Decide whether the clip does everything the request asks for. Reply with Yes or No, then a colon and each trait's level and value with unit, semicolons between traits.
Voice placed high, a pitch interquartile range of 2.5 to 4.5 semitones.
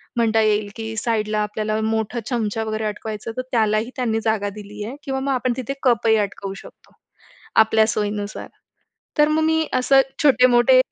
Yes: high, 220 Hz; average, 2.8 semitones